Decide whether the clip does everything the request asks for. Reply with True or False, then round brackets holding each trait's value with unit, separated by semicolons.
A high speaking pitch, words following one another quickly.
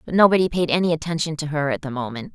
False (155 Hz; 255 wpm)